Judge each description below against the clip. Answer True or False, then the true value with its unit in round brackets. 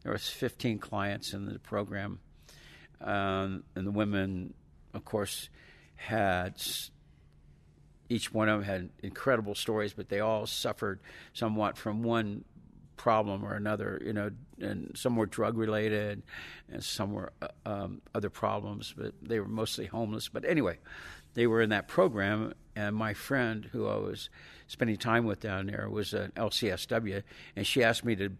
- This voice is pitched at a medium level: False (105 Hz)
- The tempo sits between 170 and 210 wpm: False (160 wpm)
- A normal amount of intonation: False (1.9 semitones)